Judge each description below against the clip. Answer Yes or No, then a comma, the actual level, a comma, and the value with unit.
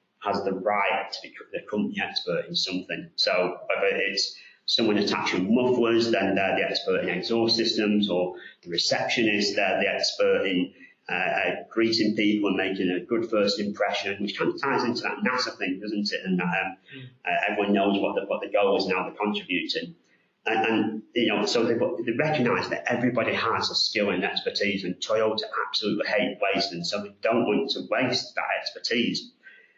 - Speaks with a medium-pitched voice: No, low, 105 Hz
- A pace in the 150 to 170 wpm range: No, average, 185 wpm